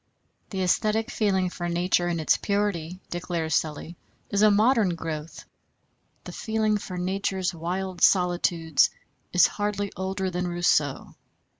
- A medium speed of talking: No, slow, 130 wpm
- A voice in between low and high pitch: Yes, medium, 180 Hz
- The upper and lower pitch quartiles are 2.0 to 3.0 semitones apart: Yes, average, 2.7 semitones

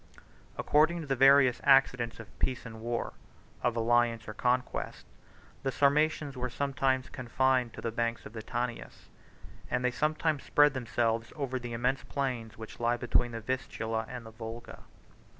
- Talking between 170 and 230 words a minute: No, average, 160 wpm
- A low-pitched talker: Yes, low, 125 Hz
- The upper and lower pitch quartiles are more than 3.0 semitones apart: No, narrow, 2.6 semitones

